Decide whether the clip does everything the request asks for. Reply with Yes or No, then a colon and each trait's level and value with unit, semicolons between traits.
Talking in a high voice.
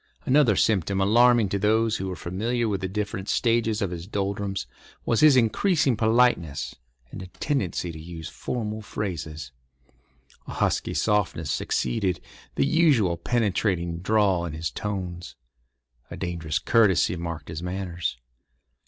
No: very low, 95 Hz